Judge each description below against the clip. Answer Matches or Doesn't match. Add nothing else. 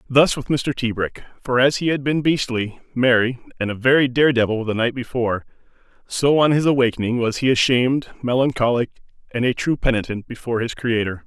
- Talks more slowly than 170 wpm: Doesn't match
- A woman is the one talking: Doesn't match